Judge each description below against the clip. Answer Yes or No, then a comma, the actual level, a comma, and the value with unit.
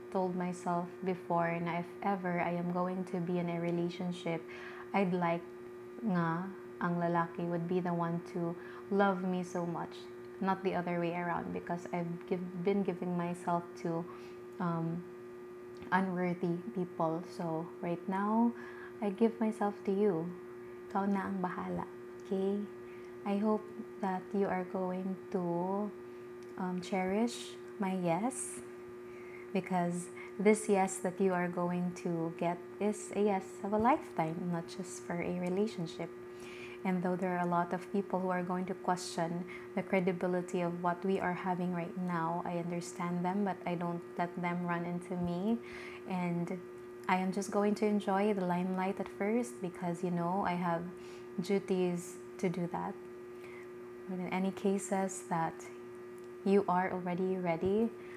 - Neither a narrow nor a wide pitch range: No, narrow, 2.0 semitones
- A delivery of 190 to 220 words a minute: No, average, 155 wpm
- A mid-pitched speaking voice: Yes, medium, 180 Hz